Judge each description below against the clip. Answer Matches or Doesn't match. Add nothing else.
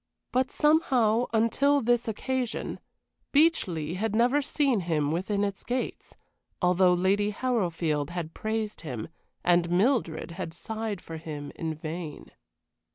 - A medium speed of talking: Doesn't match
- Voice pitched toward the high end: Matches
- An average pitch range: Doesn't match